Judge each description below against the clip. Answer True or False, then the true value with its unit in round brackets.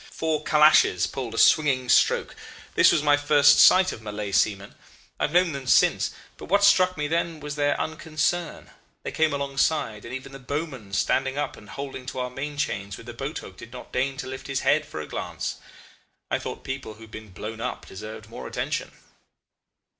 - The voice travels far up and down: False (5.0 semitones)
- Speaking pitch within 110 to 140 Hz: True (135 Hz)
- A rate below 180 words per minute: False (200 wpm)